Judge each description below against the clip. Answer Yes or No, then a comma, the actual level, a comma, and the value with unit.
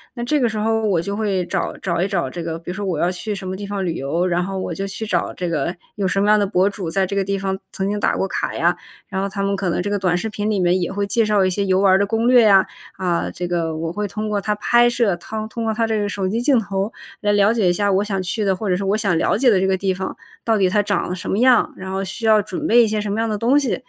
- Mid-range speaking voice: No, high, 200 Hz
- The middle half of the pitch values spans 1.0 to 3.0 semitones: Yes, narrow, 2.4 semitones